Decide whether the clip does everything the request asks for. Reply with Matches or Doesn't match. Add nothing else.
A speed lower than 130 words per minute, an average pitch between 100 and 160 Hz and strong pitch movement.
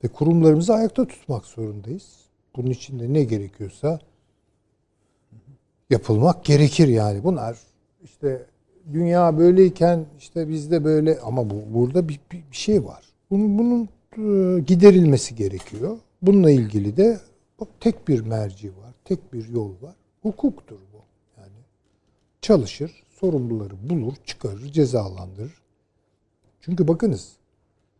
Matches